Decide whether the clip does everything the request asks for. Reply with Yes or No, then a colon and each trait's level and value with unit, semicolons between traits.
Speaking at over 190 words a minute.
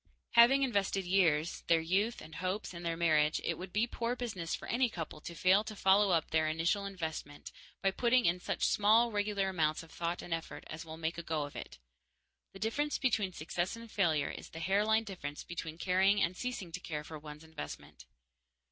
Yes: average, 200 wpm